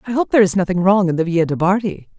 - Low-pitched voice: No, high, 190 Hz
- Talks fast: Yes, fast, 300 wpm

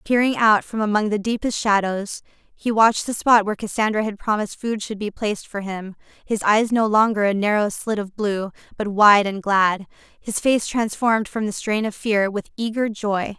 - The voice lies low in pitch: No, high, 210 Hz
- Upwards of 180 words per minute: Yes, average, 200 wpm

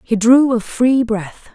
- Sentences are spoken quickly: No, average, 195 wpm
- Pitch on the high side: Yes, high, 235 Hz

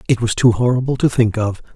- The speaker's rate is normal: No, fast, 240 wpm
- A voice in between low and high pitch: No, low, 115 Hz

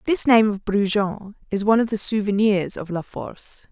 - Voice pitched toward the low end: No, high, 205 Hz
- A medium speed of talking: Yes, average, 195 wpm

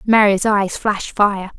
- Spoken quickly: No, average, 150 wpm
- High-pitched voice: Yes, high, 205 Hz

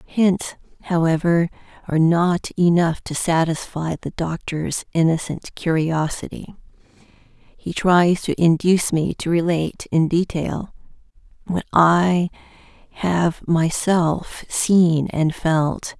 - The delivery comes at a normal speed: No, slow, 100 wpm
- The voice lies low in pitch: No, medium, 170 Hz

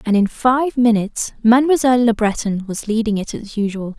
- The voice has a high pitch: Yes, high, 225 Hz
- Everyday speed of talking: Yes, average, 180 wpm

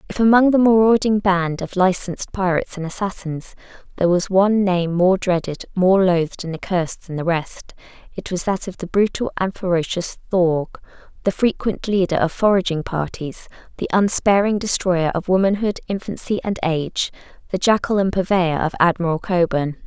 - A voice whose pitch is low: No, medium, 185 Hz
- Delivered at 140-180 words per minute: Yes, average, 155 wpm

